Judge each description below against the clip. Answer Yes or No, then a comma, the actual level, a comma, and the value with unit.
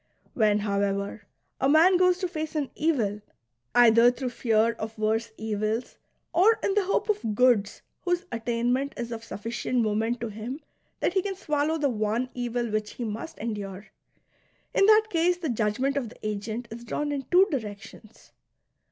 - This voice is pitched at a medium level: No, high, 240 Hz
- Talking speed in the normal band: Yes, average, 175 wpm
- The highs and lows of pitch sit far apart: Yes, wide, 5.7 semitones